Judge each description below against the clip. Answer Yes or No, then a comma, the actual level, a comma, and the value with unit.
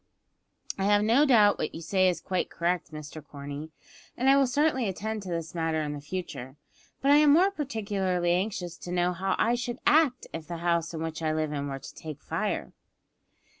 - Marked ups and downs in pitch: Yes, wide, 6.0 semitones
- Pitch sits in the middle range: Yes, medium, 180 Hz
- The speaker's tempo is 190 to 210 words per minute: Yes, average, 200 wpm